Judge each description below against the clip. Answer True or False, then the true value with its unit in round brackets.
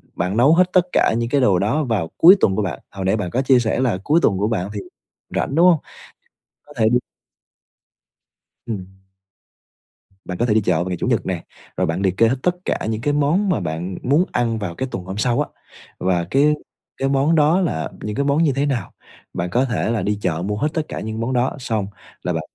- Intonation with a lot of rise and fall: True (6.5 semitones)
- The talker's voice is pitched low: True (115 Hz)